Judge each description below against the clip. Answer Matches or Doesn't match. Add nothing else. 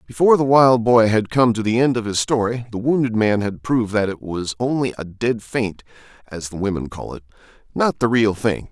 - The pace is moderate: Doesn't match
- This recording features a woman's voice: Doesn't match